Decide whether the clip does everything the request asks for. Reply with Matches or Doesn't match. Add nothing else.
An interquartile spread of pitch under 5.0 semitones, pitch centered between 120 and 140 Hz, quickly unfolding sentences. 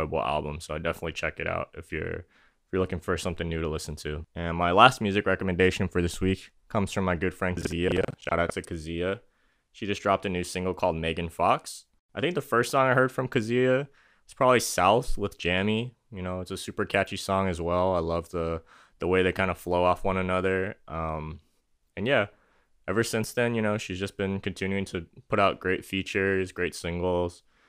Doesn't match